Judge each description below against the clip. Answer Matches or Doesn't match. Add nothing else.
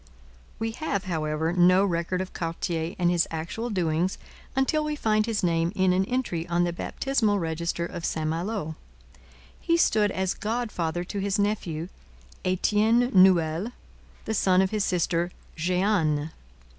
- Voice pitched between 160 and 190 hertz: Matches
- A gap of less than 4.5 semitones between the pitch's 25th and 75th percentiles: Matches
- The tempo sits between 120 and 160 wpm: Matches